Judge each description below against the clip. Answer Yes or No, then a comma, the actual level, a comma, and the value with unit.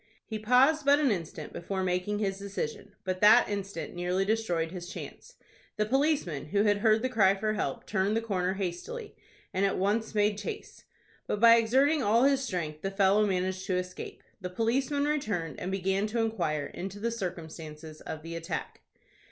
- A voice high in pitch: Yes, high, 200 Hz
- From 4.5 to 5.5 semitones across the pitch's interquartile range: No, average, 3.8 semitones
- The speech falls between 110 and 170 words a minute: No, average, 180 wpm